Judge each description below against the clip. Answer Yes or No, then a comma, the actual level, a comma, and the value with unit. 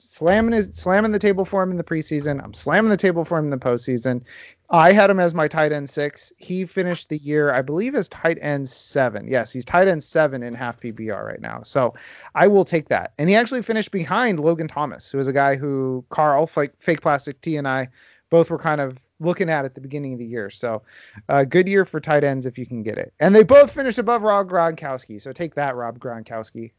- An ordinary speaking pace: No, fast, 240 wpm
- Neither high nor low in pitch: Yes, medium, 150 Hz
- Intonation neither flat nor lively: No, wide, 5.7 semitones